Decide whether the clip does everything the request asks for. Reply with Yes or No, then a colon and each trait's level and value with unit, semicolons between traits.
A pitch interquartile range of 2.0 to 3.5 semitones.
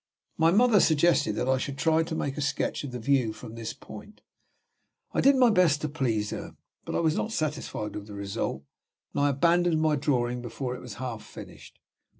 No: average, 5.1 semitones